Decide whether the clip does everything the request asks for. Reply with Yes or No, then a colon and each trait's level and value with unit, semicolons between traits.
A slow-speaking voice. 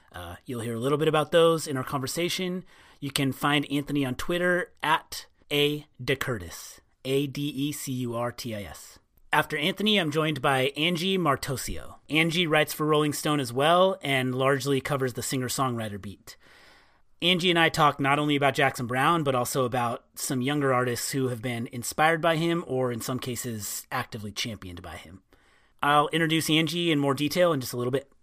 No: average, 170 wpm